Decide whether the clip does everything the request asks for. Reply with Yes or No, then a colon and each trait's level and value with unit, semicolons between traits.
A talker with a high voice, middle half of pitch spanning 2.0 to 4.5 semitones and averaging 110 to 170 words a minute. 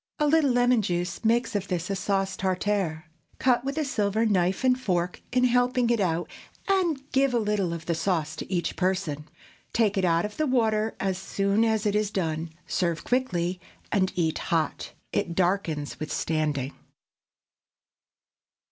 No: high, 195 Hz; wide, 5.4 semitones; average, 165 wpm